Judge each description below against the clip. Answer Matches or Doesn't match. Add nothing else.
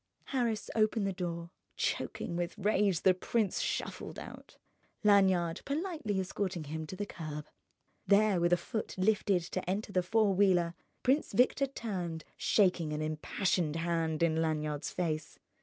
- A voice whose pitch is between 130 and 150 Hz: Doesn't match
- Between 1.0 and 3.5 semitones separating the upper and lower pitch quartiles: Doesn't match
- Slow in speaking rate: Doesn't match